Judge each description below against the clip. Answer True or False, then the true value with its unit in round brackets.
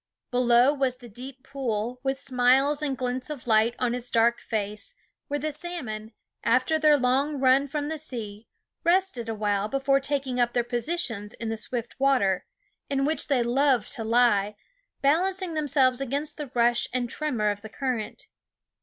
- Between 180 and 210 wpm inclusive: False (165 wpm)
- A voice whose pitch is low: False (255 Hz)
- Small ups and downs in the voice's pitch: False (3.3 semitones)